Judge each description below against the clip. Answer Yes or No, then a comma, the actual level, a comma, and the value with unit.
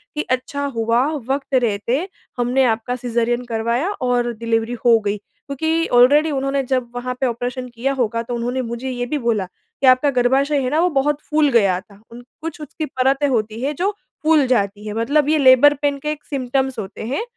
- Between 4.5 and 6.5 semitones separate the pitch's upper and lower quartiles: No, average, 3.3 semitones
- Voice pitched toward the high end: Yes, very high, 255 Hz